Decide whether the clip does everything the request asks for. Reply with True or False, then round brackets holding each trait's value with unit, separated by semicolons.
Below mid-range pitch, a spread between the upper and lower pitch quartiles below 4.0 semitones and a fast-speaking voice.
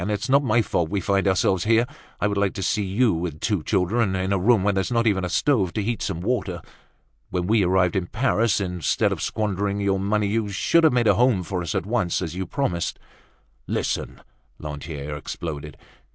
True (100 Hz; 3.6 semitones; 210 wpm)